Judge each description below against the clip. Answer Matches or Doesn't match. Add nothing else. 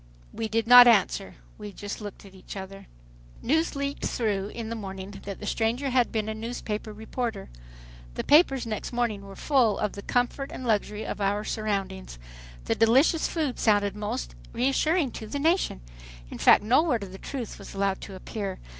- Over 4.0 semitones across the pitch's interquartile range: Doesn't match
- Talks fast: Doesn't match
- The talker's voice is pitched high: Matches